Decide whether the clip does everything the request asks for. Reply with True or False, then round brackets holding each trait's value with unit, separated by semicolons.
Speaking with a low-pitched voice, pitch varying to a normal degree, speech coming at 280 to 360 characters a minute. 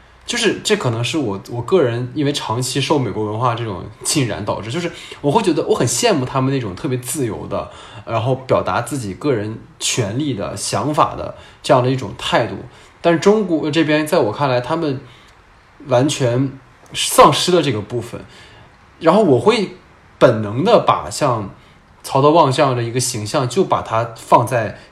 False (130 Hz; 4.1 semitones; 265 characters per minute)